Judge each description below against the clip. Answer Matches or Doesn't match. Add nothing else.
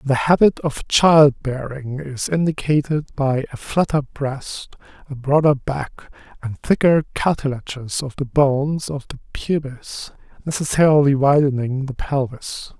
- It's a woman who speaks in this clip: Doesn't match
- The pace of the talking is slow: Matches